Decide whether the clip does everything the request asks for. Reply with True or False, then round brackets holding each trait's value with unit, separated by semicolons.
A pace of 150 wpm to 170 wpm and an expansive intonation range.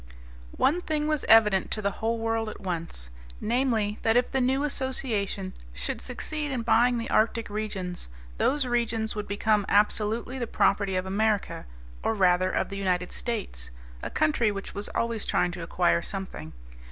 False (165 wpm; 3.7 semitones)